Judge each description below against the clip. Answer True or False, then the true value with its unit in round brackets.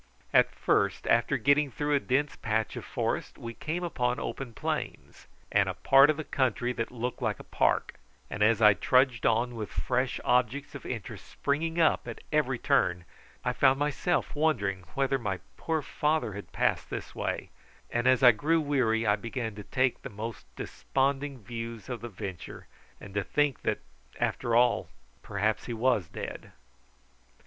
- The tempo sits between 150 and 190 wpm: True (175 wpm)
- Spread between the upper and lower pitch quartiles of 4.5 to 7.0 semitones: False (4.0 semitones)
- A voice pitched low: True (125 Hz)